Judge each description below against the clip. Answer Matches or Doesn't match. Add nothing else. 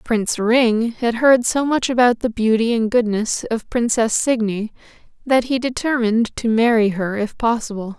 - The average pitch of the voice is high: Matches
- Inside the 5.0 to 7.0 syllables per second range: Doesn't match